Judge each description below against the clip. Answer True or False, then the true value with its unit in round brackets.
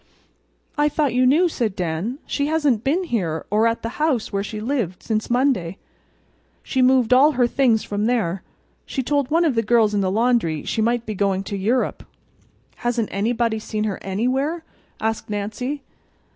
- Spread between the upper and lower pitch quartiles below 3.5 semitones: False (4.2 semitones)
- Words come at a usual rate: True (175 wpm)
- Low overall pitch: False (230 Hz)